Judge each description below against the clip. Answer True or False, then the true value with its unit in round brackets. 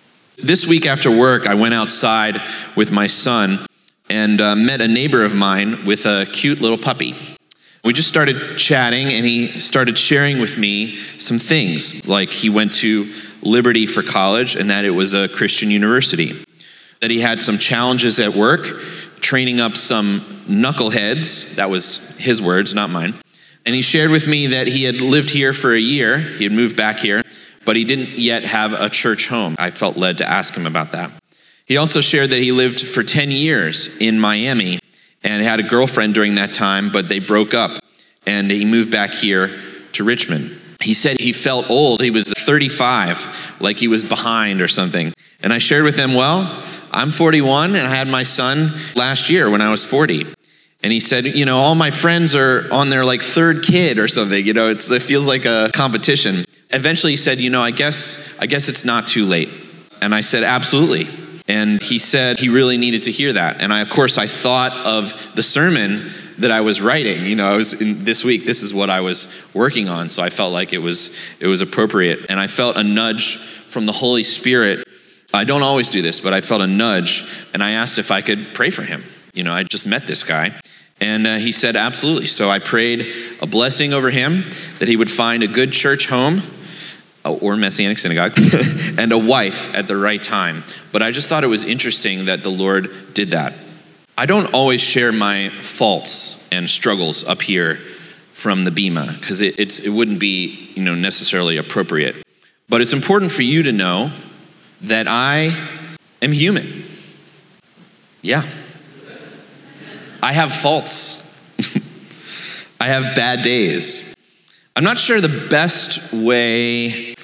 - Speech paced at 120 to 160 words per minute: False (190 wpm)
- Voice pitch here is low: True (120 Hz)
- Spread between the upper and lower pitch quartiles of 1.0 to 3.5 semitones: False (4.6 semitones)